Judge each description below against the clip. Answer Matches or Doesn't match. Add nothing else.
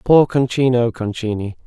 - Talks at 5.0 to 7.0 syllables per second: Doesn't match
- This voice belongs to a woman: Doesn't match